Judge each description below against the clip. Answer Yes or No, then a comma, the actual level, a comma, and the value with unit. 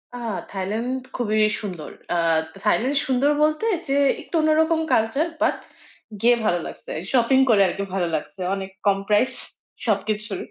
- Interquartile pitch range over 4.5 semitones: Yes, average, 5.1 semitones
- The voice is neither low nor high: No, high, 220 Hz